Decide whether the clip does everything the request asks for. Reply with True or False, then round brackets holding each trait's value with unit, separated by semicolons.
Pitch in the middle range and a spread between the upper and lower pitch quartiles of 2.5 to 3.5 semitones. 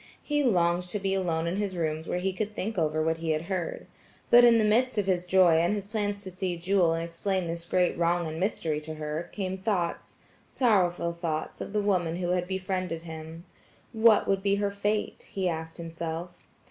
True (180 Hz; 3.1 semitones)